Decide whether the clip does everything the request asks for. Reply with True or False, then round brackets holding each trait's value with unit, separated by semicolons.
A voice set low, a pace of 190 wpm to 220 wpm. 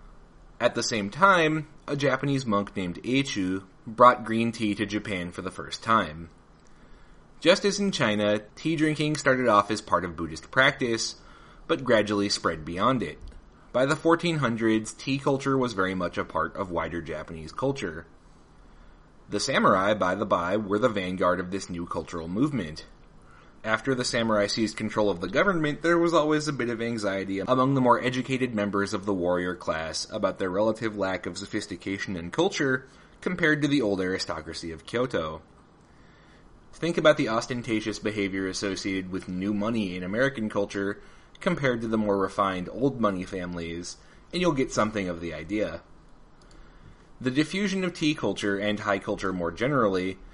False (105 Hz; 165 wpm)